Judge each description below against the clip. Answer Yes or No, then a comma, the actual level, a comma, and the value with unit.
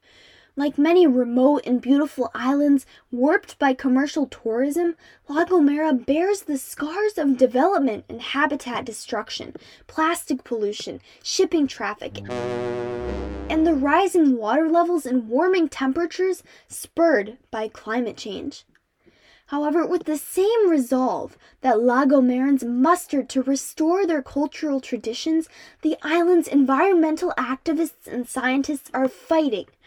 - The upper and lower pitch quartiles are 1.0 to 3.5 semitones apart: No, average, 4.3 semitones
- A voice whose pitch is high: Yes, very high, 285 Hz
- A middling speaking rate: No, slow, 115 wpm